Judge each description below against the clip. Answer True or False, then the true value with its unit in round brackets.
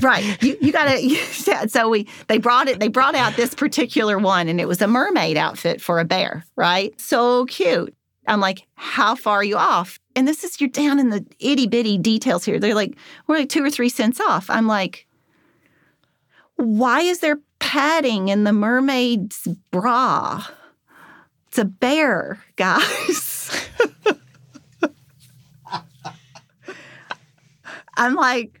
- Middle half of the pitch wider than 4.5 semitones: True (5.2 semitones)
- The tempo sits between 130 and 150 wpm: True (145 wpm)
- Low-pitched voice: False (235 Hz)